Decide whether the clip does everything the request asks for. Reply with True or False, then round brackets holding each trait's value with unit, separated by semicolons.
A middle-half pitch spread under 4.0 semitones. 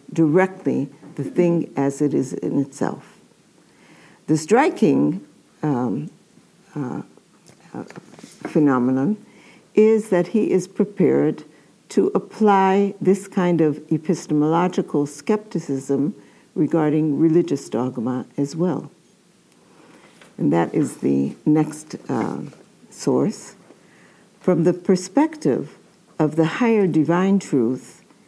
False (4.8 semitones)